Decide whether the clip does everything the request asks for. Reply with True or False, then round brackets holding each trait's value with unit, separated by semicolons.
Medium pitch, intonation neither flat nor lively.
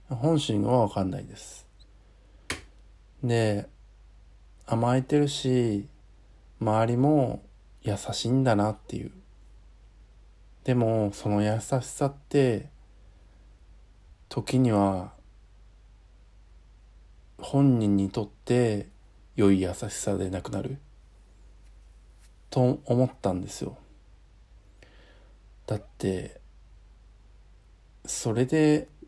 False (105 Hz; 4.1 semitones)